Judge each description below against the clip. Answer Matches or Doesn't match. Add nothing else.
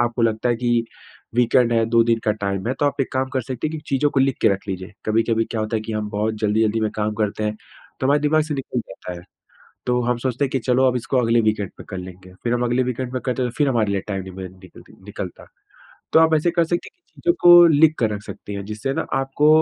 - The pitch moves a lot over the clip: Doesn't match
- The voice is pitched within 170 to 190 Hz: Doesn't match